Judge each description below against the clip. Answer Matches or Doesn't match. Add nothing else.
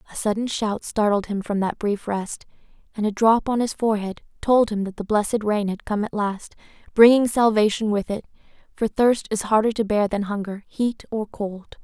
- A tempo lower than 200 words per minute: Doesn't match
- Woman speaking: Matches